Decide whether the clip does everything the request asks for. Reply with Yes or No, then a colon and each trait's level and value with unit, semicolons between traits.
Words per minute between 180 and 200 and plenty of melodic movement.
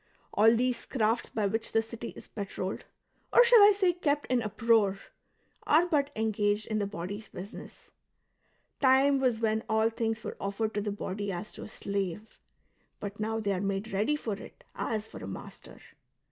No: average, 190 wpm; average, 3.0 semitones